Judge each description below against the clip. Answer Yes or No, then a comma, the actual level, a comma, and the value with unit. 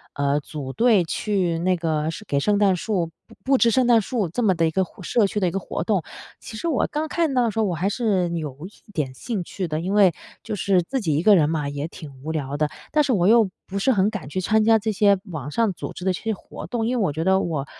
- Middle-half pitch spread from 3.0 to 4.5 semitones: No, average, 5.3 semitones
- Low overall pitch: No, high, 190 Hz